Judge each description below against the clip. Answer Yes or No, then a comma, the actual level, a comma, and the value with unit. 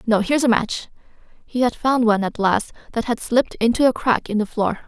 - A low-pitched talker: No, high, 230 Hz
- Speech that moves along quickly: Yes, fast, 235 wpm